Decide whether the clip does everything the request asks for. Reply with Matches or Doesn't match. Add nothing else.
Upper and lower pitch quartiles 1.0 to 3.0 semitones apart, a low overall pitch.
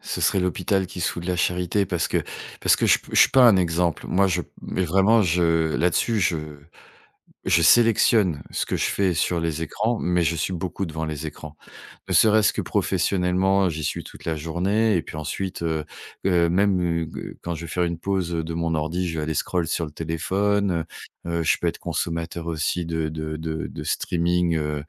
Matches